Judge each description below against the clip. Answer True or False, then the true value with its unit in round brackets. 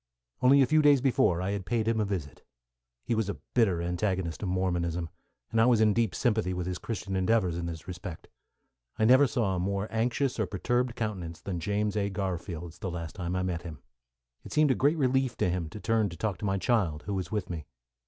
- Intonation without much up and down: False (4.5 semitones)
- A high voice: False (100 Hz)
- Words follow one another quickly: True (225 wpm)